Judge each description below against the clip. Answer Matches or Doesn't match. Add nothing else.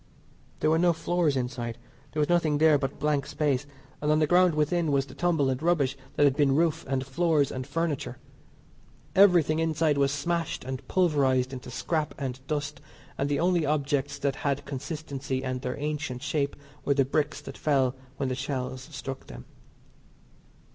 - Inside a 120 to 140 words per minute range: Doesn't match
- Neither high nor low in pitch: Matches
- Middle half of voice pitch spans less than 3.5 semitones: Matches